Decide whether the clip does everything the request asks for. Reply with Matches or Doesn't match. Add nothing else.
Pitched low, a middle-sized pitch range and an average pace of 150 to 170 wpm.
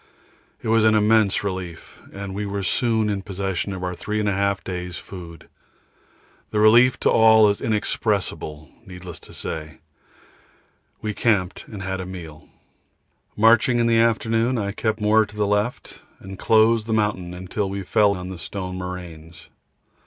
Matches